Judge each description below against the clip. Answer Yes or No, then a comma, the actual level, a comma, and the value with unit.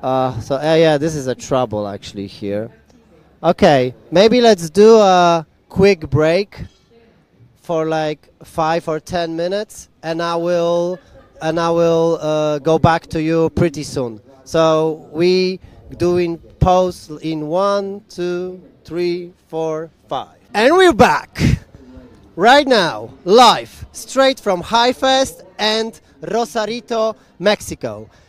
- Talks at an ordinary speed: No, slow, 125 wpm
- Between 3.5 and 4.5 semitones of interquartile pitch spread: Yes, average, 3.8 semitones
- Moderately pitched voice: Yes, medium, 165 Hz